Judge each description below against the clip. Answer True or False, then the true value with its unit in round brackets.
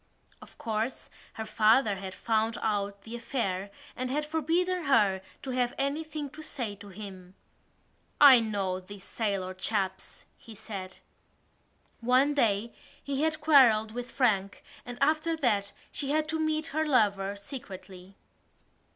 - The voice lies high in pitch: True (225 Hz)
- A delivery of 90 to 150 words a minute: True (140 wpm)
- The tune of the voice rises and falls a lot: True (5.9 semitones)